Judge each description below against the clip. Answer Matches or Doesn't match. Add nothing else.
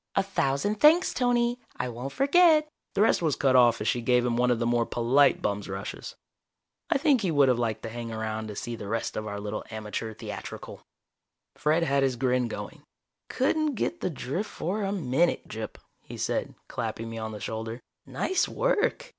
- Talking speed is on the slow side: Doesn't match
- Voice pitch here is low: Matches